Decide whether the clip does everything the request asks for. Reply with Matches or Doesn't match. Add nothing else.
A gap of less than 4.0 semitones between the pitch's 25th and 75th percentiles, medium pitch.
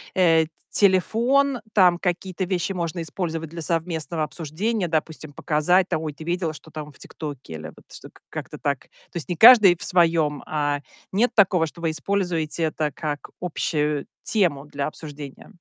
Matches